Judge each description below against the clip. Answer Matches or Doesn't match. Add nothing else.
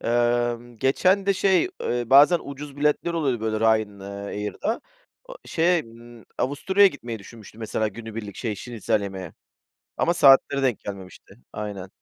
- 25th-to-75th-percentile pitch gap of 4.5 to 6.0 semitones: Matches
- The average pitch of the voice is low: Matches